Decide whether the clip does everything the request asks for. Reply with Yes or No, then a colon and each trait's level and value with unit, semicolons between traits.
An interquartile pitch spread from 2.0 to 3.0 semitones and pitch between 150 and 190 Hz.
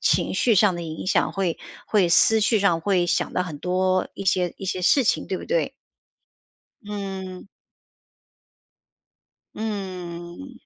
Yes: average, 2.7 semitones; medium, 185 Hz